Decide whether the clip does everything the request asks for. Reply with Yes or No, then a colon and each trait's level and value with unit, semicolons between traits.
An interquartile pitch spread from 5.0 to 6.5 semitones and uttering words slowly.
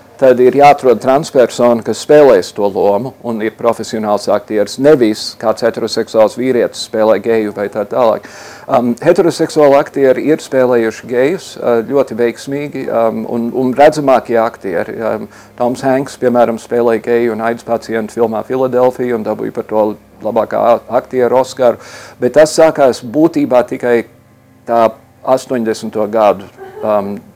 No: average, 2.8 semitones; slow, 130 wpm